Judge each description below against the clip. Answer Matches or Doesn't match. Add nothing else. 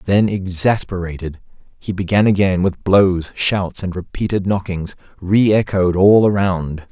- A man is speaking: Matches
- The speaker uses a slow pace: Matches